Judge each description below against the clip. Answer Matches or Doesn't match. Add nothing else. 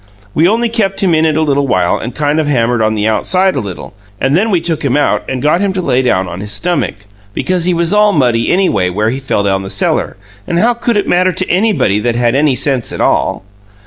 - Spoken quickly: Matches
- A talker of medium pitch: Matches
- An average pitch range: Doesn't match